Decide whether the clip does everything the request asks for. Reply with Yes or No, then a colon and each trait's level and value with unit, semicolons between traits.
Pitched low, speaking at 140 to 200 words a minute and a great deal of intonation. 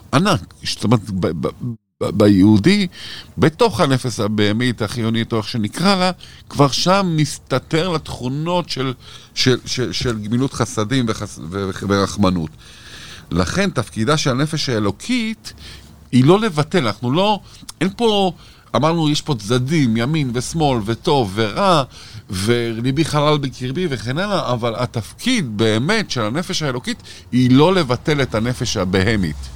No: low, 125 Hz; average, 125 wpm; wide, 6.1 semitones